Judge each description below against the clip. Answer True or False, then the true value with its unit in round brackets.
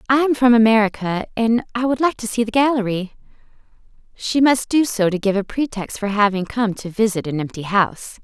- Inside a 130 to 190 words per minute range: False (205 wpm)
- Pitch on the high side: True (220 Hz)